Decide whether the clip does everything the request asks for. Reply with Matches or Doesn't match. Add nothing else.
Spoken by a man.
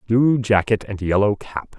Matches